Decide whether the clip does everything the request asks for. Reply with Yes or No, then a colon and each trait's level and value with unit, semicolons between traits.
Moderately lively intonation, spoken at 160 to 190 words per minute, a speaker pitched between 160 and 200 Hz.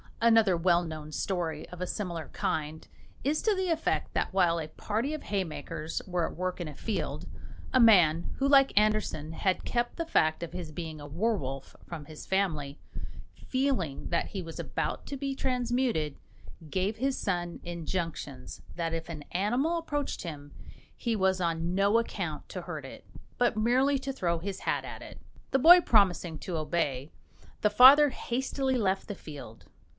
No: wide, 6.8 semitones; average, 170 wpm; medium, 185 Hz